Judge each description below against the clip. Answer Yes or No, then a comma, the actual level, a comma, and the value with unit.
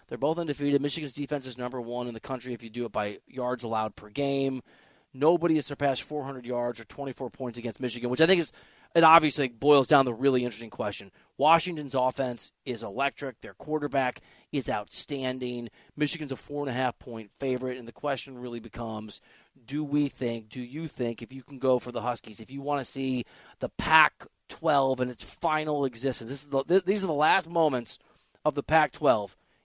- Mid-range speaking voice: No, low, 130 Hz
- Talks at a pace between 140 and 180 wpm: No, average, 200 wpm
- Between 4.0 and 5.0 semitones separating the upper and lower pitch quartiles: No, average, 3.2 semitones